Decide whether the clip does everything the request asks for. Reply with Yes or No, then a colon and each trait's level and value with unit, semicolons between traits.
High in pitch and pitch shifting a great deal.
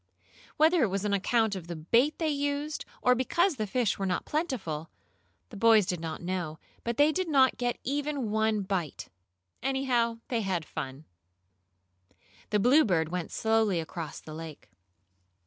Yes: high, 220 Hz; wide, 7.0 semitones